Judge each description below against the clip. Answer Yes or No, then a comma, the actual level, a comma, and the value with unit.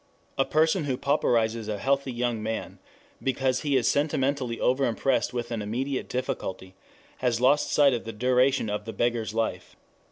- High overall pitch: No, low, 125 Hz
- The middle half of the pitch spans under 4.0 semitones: Yes, average, 3.1 semitones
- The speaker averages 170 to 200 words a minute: No, average, 160 wpm